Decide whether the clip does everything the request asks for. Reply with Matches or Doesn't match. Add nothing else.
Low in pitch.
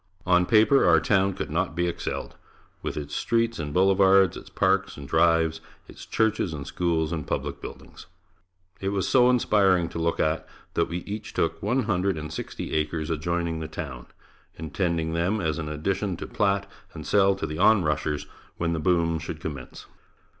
Matches